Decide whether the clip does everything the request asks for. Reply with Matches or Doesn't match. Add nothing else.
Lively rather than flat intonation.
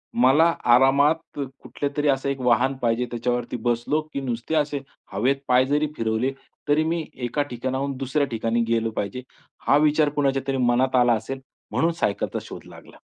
Doesn't match